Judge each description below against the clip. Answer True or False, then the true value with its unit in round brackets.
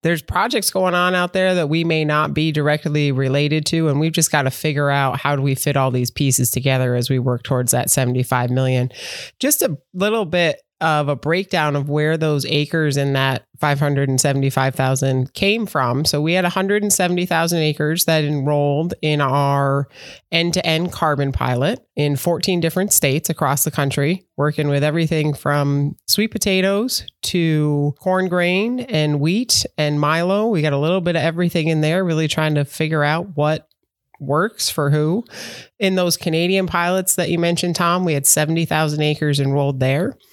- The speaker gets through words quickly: False (175 wpm)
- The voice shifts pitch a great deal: False (3.6 semitones)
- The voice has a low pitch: False (155 Hz)